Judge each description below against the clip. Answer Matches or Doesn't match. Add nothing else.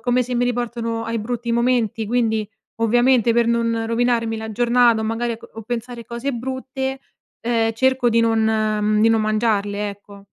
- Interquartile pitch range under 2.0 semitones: Matches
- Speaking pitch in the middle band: Doesn't match